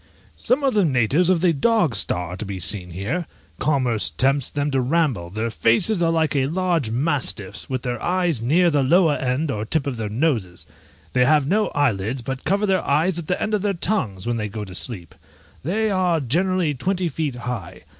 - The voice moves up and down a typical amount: No, wide, 7.2 semitones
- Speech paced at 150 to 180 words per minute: No, fast, 205 wpm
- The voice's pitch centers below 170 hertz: Yes, medium, 140 Hz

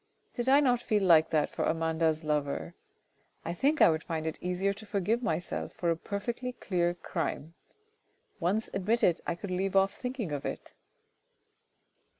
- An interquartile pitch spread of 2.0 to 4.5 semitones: No, average, 5.1 semitones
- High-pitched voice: No, medium, 180 Hz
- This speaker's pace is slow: No, average, 160 wpm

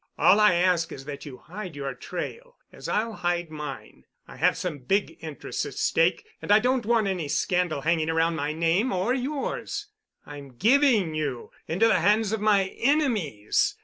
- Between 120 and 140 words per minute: No, average, 175 wpm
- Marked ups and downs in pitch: Yes, wide, 6.1 semitones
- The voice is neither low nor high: Yes, medium, 180 Hz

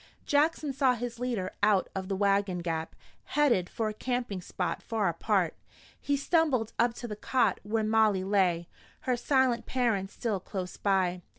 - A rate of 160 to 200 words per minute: Yes, average, 165 wpm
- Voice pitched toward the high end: Yes, high, 215 Hz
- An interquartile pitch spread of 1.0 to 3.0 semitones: No, average, 4.5 semitones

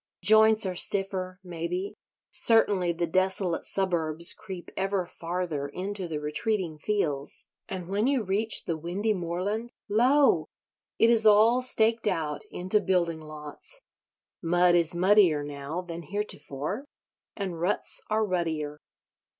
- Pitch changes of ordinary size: Yes, average, 4.0 semitones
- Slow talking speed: Yes, slow, 125 wpm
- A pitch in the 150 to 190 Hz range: Yes, medium, 185 Hz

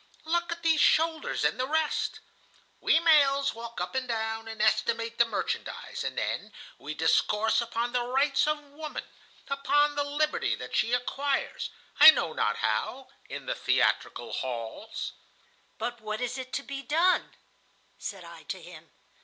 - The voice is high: Yes, very high, 255 Hz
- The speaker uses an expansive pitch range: No, average, 4.9 semitones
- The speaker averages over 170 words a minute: No, average, 155 wpm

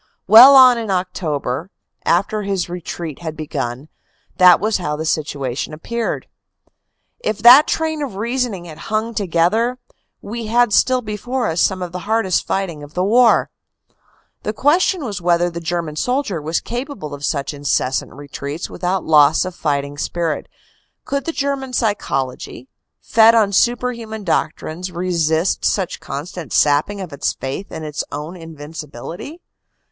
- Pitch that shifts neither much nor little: No, wide, 6.6 semitones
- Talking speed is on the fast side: No, average, 150 wpm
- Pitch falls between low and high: Yes, medium, 180 Hz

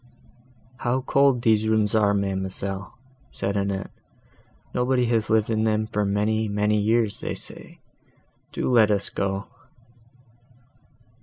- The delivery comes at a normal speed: No, slow, 125 wpm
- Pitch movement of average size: No, narrow, 1.9 semitones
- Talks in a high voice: No, low, 105 Hz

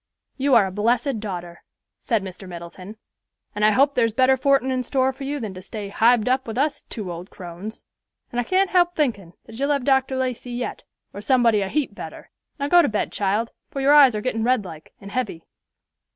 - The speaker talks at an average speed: No, fast, 215 wpm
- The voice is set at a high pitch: Yes, high, 235 Hz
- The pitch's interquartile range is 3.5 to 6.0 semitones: Yes, average, 4.8 semitones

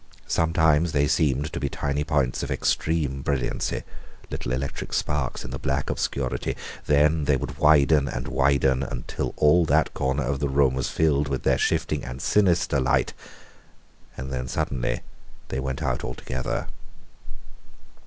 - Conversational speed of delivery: Yes, average, 150 wpm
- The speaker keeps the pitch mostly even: Yes, narrow, 2.1 semitones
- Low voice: Yes, very low, 70 Hz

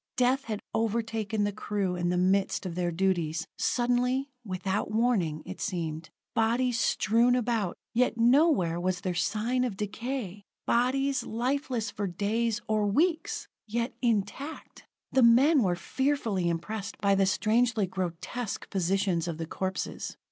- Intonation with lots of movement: No, average, 4.7 semitones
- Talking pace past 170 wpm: No, average, 140 wpm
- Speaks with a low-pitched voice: No, high, 215 Hz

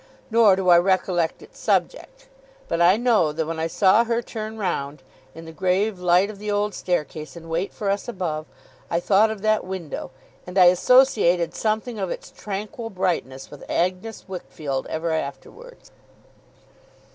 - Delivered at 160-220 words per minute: Yes, average, 165 wpm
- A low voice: No, medium, 185 Hz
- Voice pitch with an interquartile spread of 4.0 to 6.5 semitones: Yes, average, 4.3 semitones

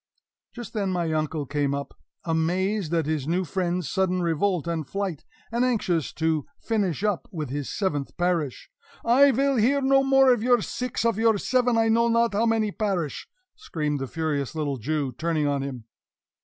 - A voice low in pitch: No, medium, 180 Hz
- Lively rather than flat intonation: Yes, wide, 6.6 semitones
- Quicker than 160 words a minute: Yes, average, 180 wpm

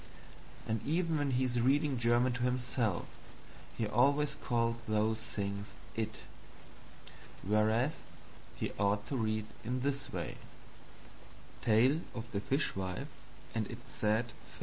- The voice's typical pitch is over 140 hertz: No, low, 115 Hz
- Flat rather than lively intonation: No, average, 3.2 semitones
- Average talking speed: No, slow, 130 wpm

